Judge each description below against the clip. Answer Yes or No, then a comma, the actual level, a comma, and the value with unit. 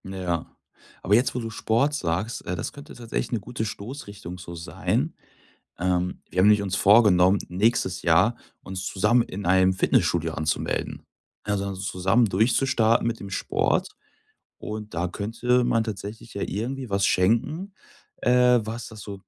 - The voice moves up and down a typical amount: Yes, average, 4.0 semitones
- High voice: No, low, 105 Hz